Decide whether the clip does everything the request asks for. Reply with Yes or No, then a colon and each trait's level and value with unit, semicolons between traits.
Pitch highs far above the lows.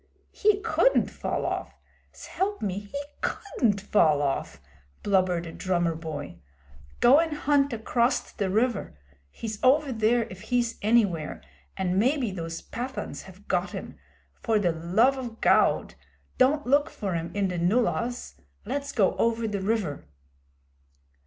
Yes: wide, 5.9 semitones